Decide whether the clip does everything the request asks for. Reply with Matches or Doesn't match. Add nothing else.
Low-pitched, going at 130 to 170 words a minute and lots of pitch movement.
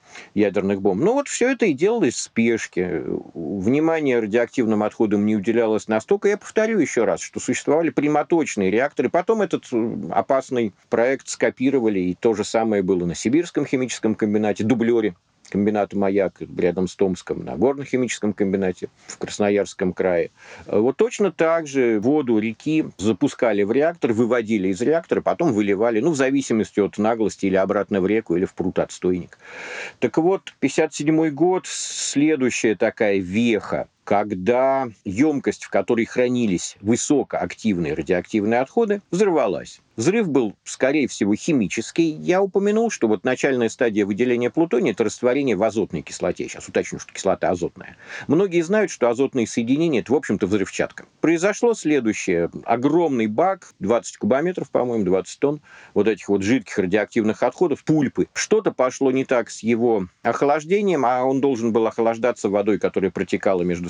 Matches